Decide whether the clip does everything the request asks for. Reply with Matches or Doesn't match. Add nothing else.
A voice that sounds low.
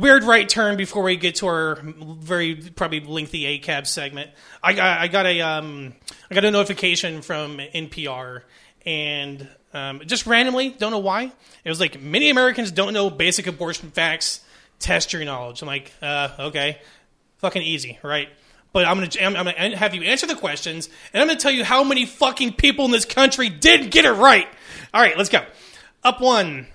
Doesn't match